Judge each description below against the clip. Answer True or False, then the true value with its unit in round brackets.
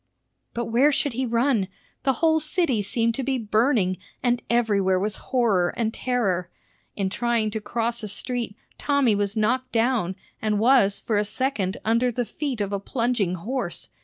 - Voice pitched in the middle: False (230 Hz)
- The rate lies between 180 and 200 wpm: False (170 wpm)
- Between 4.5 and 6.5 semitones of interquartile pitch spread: False (3.6 semitones)